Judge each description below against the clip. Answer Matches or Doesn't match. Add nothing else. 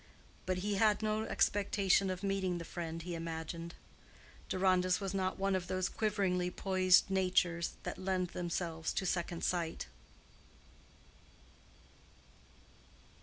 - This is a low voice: Doesn't match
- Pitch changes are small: Matches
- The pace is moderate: Doesn't match